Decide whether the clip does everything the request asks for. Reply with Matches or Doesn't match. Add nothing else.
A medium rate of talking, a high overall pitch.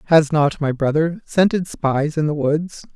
Doesn't match